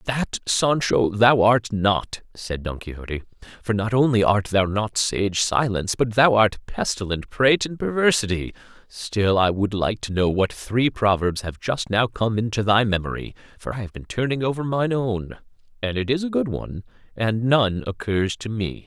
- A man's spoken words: Yes, male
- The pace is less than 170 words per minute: No, average, 180 wpm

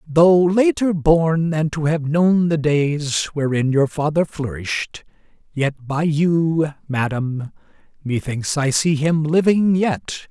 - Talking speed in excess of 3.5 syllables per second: No, 3.4 syllables/s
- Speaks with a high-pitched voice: No, medium, 155 Hz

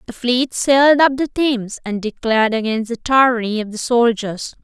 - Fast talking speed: No, average, 180 wpm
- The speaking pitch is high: Yes, high, 240 Hz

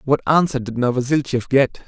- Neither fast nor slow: Yes, average, 160 wpm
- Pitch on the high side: No, low, 130 Hz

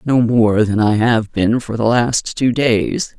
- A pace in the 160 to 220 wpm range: Yes, fast, 205 wpm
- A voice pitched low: Yes, low, 115 Hz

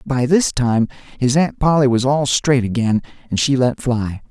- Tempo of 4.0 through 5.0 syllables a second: Yes, 4.5 syllables/s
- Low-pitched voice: Yes, low, 130 Hz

